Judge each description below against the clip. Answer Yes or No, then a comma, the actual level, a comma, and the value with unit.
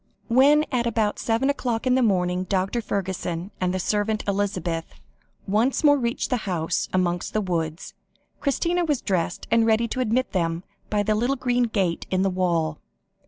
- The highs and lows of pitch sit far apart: No, average, 4.9 semitones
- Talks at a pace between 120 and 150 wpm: No, average, 170 wpm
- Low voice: No, high, 210 Hz